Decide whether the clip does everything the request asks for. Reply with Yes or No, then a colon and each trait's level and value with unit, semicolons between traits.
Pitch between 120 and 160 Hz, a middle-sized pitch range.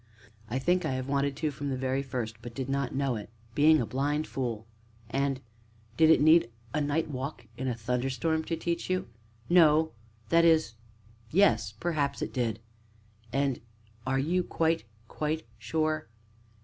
Yes: medium, 140 Hz; average, 3.6 semitones